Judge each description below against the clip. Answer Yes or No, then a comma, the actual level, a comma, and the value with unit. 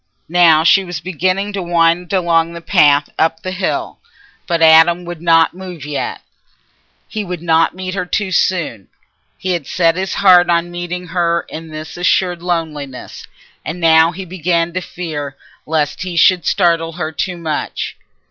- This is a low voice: No, medium, 170 Hz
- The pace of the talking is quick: No, average, 165 wpm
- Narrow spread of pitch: Yes, narrow, 1.9 semitones